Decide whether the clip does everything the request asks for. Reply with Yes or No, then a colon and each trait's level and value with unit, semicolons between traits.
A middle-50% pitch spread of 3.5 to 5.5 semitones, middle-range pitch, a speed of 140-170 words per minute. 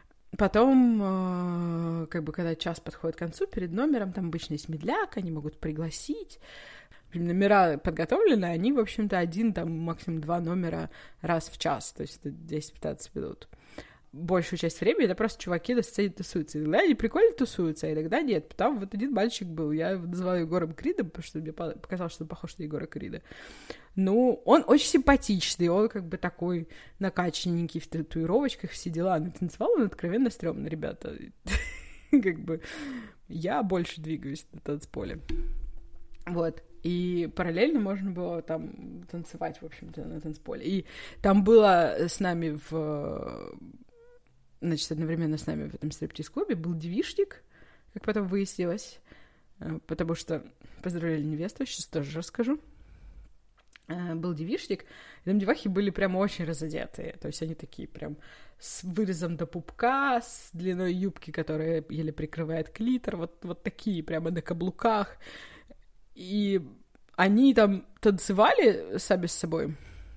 Yes: average, 4.1 semitones; medium, 175 Hz; average, 145 wpm